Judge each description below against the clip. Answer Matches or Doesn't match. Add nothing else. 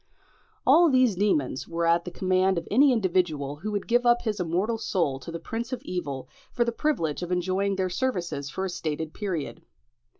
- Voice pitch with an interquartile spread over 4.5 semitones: Matches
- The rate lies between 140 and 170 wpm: Doesn't match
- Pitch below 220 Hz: Matches